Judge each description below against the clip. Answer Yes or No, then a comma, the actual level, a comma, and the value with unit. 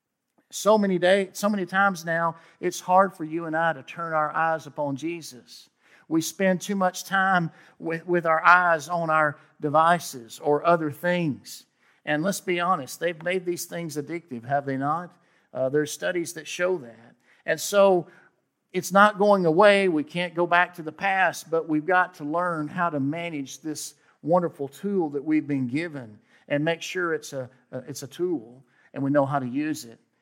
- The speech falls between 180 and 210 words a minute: Yes, average, 190 wpm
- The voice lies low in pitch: No, medium, 165 Hz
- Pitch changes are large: No, average, 3.3 semitones